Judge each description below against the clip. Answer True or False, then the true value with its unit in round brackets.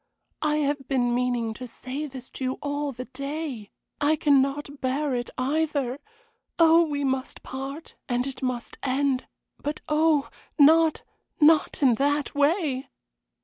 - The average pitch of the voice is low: False (280 Hz)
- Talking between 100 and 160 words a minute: True (145 wpm)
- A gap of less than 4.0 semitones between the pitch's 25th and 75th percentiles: True (2.6 semitones)